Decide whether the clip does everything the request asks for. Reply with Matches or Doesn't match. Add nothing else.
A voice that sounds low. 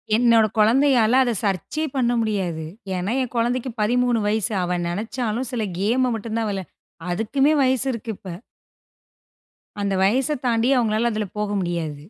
Doesn't match